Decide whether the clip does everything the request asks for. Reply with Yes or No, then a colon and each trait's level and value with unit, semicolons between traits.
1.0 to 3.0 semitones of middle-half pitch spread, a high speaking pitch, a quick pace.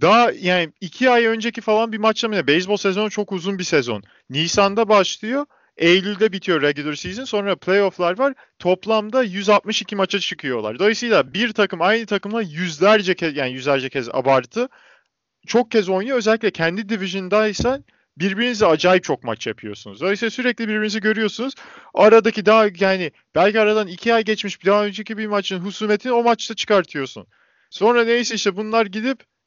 No: average, 3.7 semitones; high, 210 Hz; fast, 155 wpm